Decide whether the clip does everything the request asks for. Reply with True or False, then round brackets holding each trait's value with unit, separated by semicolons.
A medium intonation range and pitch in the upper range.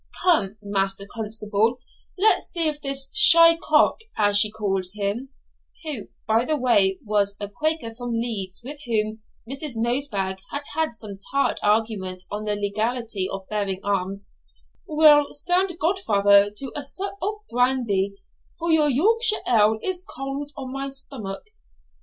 False (6.3 semitones; 230 Hz)